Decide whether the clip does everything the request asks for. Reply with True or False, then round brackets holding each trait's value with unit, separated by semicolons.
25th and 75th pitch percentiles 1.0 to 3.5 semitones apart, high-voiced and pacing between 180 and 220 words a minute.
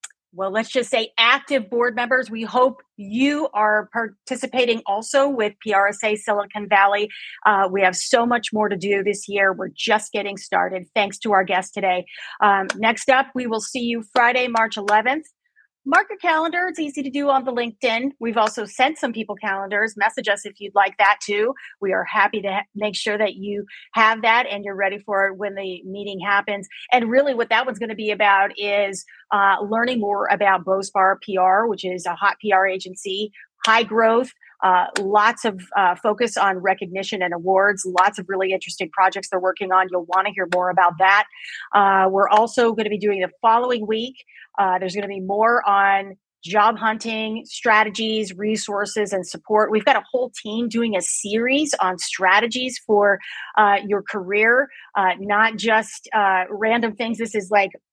True (2.9 semitones; 210 Hz; 190 wpm)